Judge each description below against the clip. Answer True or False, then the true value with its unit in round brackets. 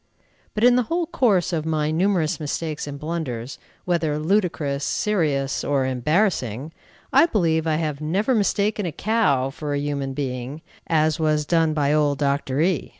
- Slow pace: False (160 wpm)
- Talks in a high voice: False (155 Hz)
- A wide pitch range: False (4.2 semitones)